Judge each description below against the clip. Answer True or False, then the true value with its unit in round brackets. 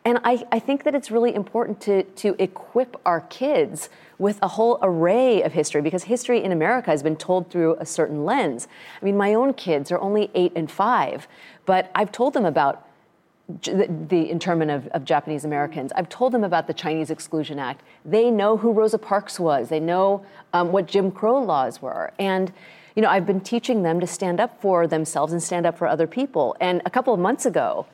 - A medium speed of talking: False (210 wpm)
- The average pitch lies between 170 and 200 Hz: True (190 Hz)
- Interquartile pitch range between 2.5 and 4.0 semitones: False (5.1 semitones)